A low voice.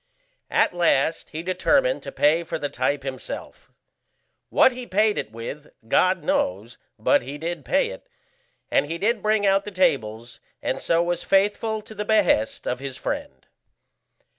No: medium, 170 Hz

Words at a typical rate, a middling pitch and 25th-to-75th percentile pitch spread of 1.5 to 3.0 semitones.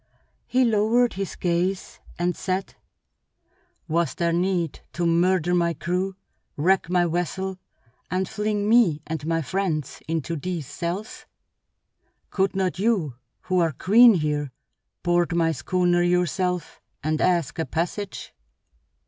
No: slow, 125 wpm; medium, 175 Hz; narrow, 2.4 semitones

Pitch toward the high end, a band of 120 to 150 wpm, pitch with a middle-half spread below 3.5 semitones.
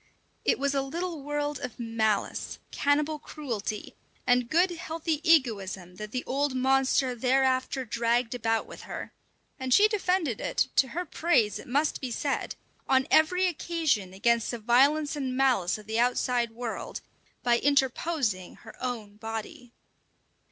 No: very high, 255 Hz; average, 145 wpm; average, 4.2 semitones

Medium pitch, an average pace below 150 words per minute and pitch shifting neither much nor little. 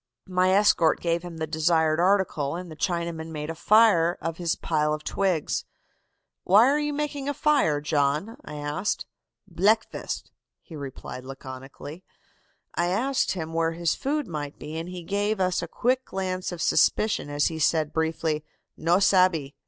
No: medium, 170 Hz; average, 165 wpm; average, 4.0 semitones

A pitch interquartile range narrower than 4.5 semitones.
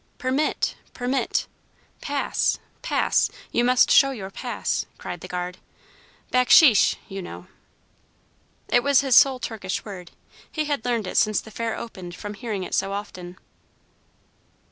No: average, 5.1 semitones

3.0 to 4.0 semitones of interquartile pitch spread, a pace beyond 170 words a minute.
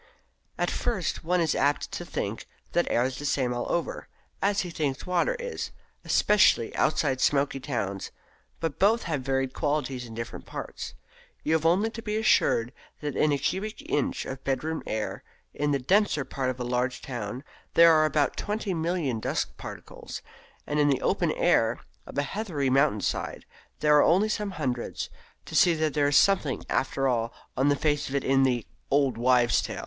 No: average, 4.5 semitones; average, 185 wpm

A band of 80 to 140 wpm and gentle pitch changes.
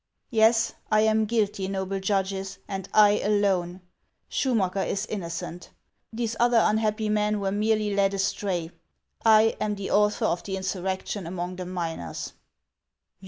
Yes: slow, 135 wpm; narrow, 2.1 semitones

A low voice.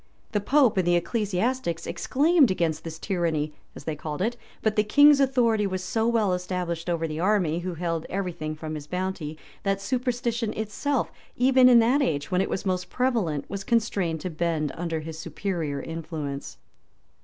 No: medium, 185 Hz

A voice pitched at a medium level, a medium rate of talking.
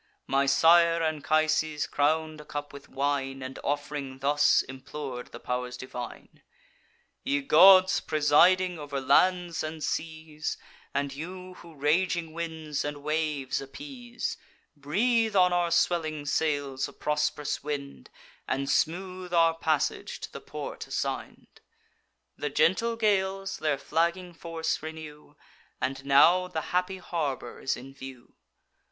No: medium, 155 Hz; slow, 125 wpm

